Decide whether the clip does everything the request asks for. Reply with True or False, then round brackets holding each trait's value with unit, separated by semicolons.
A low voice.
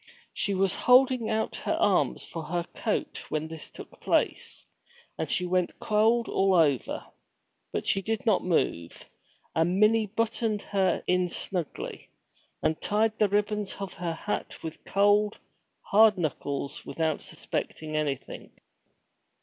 False (195 Hz)